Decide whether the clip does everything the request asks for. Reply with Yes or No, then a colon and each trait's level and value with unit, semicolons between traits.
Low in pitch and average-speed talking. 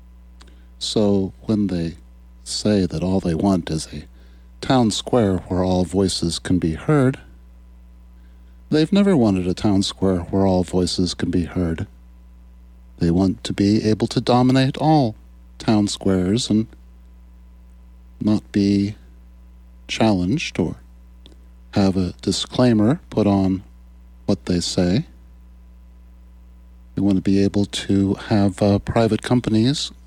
No: very low, 90 Hz; slow, 125 wpm